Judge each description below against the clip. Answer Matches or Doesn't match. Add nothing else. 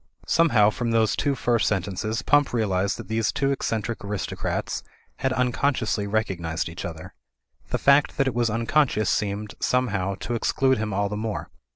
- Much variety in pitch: Doesn't match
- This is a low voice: Matches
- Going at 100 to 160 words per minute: Doesn't match